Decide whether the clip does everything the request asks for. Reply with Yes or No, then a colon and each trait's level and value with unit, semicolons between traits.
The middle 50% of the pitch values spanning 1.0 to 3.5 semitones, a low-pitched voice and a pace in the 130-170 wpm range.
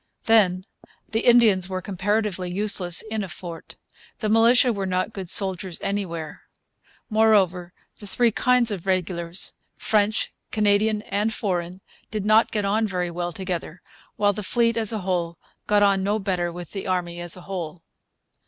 No: average, 3.1 semitones; high, 195 Hz; average, 160 wpm